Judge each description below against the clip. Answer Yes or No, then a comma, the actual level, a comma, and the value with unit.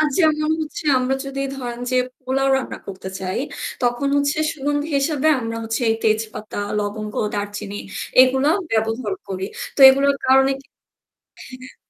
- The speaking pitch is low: No, very high, 255 Hz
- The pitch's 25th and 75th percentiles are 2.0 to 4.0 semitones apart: No, average, 4.4 semitones